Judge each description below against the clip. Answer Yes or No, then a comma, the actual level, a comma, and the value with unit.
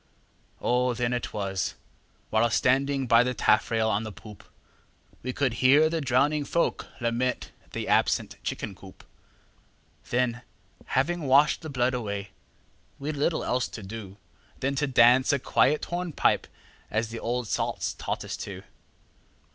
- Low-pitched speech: Yes, low, 125 Hz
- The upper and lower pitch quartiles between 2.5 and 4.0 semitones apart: Yes, average, 3.3 semitones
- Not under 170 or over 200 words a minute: No, average, 145 wpm